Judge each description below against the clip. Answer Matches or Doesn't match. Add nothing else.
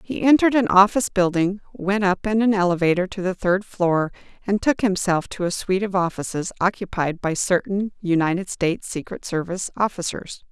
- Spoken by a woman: Matches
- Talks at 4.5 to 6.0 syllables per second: Matches